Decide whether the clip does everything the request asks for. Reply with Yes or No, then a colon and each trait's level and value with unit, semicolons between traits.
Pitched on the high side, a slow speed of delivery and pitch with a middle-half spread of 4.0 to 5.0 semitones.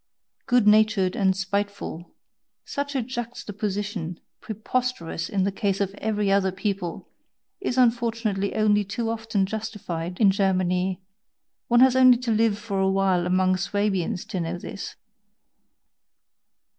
No: high, 200 Hz; slow, 130 wpm; average, 2.9 semitones